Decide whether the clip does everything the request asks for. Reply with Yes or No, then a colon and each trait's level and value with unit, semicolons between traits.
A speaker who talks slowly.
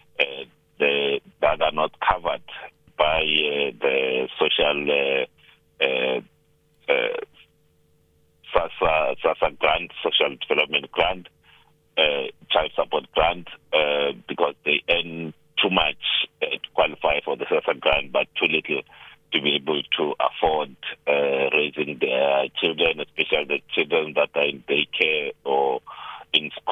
Yes: slow, 125 wpm